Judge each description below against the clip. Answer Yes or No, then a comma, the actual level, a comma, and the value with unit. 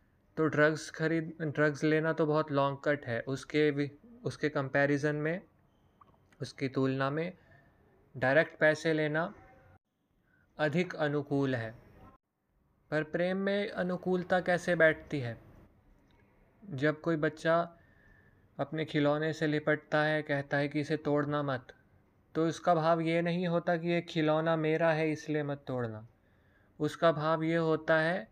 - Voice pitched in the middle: Yes, medium, 150 Hz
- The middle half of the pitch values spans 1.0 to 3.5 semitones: Yes, average, 3.0 semitones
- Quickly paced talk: No, average, 135 wpm